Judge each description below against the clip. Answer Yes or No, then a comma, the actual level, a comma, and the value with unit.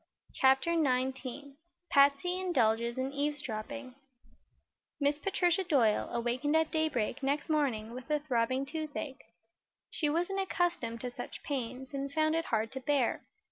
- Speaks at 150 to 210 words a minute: No, slow, 135 wpm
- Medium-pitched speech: No, very high, 280 Hz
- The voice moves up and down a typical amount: Yes, average, 3.7 semitones